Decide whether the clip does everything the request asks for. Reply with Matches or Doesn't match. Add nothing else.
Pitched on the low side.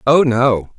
Matches